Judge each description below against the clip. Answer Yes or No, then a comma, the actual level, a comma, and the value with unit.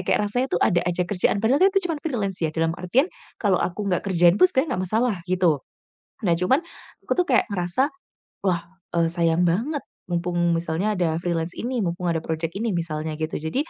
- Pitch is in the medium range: Yes, medium, 180 Hz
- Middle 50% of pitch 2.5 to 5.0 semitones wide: No, wide, 5.4 semitones